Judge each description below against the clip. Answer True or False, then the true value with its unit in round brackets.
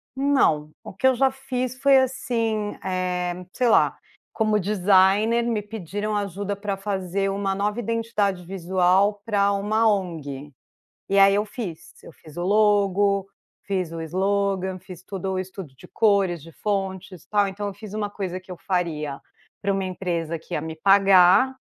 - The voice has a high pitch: True (195 Hz)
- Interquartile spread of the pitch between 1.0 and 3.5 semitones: True (2.4 semitones)